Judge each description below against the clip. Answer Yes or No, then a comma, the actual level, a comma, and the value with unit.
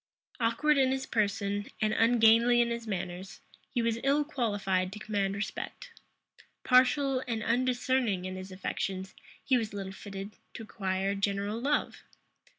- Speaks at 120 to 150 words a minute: Yes, average, 145 wpm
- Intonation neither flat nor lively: Yes, average, 4.0 semitones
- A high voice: Yes, high, 220 Hz